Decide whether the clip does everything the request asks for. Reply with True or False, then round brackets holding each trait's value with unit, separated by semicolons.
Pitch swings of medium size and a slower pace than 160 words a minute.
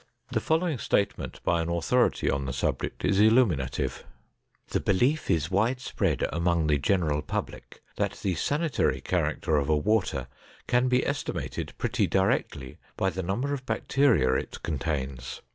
False (8.9 semitones; 145 wpm)